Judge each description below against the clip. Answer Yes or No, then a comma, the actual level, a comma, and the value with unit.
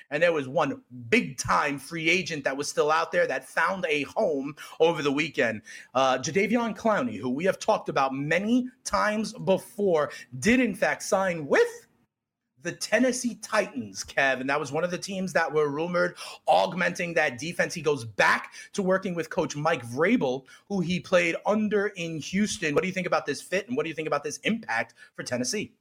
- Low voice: No, medium, 175 Hz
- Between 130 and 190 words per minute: No, average, 200 wpm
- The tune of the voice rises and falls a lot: Yes, wide, 6.1 semitones